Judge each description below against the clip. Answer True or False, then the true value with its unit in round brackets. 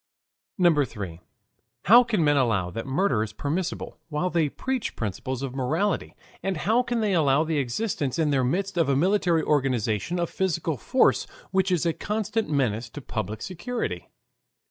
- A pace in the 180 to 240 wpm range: False (165 wpm)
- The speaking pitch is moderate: True (155 Hz)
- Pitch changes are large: True (6.7 semitones)